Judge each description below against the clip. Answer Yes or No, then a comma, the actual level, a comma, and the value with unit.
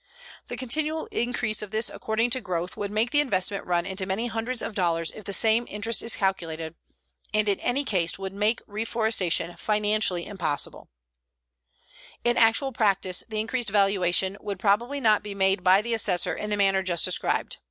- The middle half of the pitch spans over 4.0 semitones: No, average, 3.1 semitones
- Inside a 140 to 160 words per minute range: No, average, 175 wpm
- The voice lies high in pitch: Yes, high, 210 Hz